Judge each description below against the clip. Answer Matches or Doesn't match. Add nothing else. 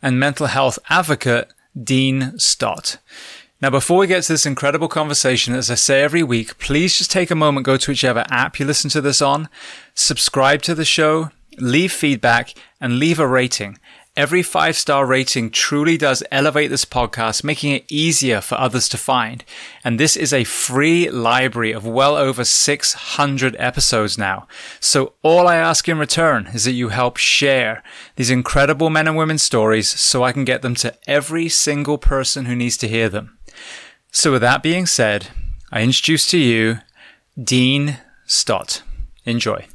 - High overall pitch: Doesn't match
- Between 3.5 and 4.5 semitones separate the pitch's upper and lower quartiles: Matches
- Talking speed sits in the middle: Matches